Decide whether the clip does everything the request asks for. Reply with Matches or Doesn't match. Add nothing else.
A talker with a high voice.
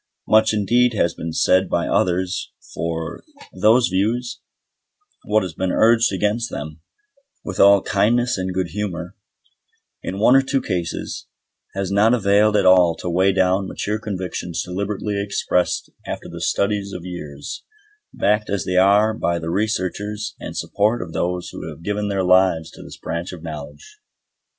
Doesn't match